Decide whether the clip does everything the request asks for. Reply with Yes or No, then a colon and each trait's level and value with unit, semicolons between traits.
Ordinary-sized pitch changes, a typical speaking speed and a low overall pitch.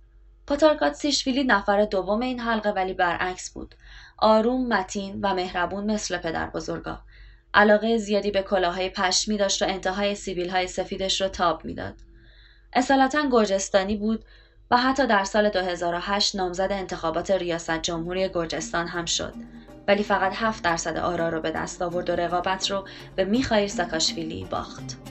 No: average, 3.0 semitones; average, 145 wpm; high, 190 Hz